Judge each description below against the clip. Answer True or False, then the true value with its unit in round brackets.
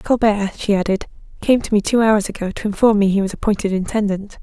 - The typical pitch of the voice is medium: False (205 Hz)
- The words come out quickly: True (215 wpm)